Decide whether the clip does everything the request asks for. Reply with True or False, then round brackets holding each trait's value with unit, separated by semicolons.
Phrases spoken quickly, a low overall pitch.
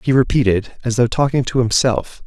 False (185 wpm; 120 Hz)